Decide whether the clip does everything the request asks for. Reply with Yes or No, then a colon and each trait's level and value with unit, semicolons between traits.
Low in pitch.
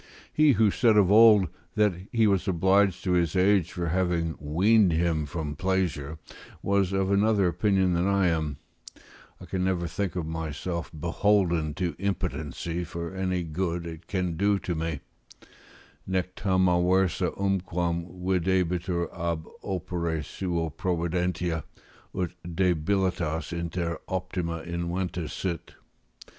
Yes: very low, 90 Hz